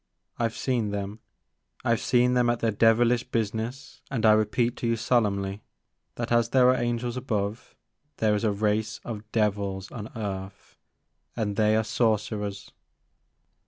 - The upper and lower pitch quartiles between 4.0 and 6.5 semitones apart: No, narrow, 2.4 semitones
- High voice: No, low, 110 Hz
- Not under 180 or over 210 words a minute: No, average, 165 wpm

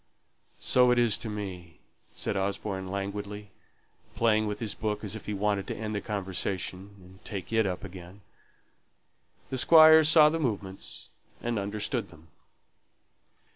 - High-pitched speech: No, low, 105 Hz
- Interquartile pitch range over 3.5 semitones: No, average, 2.7 semitones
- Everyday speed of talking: Yes, average, 145 wpm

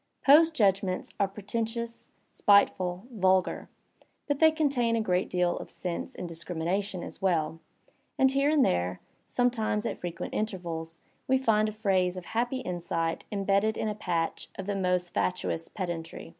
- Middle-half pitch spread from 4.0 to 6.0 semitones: Yes, average, 4.4 semitones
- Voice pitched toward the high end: Yes, high, 195 Hz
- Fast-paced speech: No, average, 155 wpm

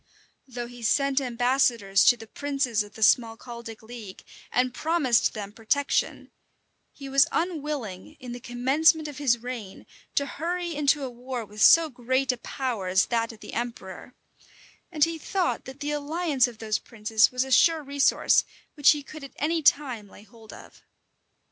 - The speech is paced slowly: No, average, 170 wpm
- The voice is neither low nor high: No, very high, 255 Hz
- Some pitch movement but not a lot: Yes, average, 4.1 semitones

